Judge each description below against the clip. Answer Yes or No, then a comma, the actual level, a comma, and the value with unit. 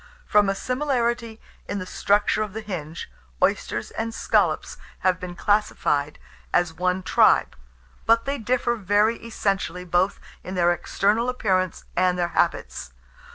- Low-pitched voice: No, high, 200 Hz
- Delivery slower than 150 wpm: Yes, average, 140 wpm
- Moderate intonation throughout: Yes, average, 3.9 semitones